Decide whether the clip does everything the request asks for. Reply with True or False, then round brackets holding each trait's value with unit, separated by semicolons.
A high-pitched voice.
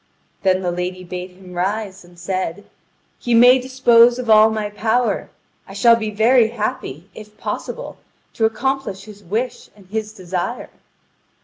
True (215 Hz)